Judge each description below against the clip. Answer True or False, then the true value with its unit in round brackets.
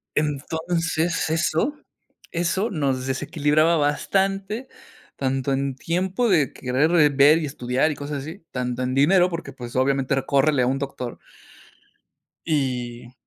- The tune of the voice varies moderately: True (3.9 semitones)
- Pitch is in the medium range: True (145 Hz)